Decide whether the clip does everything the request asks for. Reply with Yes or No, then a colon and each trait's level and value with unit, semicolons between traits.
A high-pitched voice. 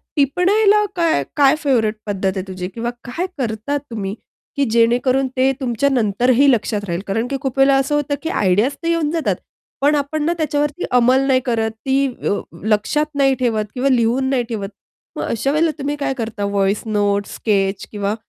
Yes: very high, 255 Hz